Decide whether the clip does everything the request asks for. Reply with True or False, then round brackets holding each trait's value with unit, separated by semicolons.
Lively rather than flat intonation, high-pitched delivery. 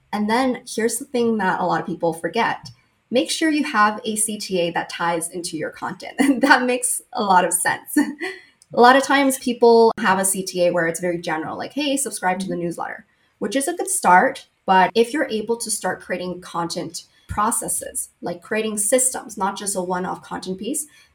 True (6.0 semitones; 215 Hz)